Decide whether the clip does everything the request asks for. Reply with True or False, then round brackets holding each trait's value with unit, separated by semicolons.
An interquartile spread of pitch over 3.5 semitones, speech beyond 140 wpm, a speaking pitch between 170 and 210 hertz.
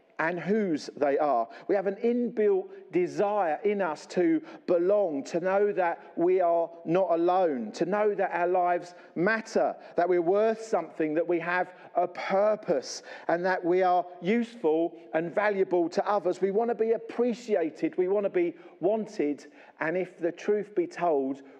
True (4.0 semitones; 165 wpm; 190 Hz)